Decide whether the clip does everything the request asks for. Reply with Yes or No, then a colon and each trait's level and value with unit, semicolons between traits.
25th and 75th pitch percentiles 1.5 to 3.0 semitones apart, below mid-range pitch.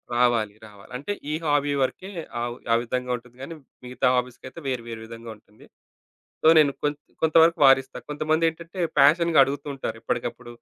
No: average, 4.3 semitones; low, 130 Hz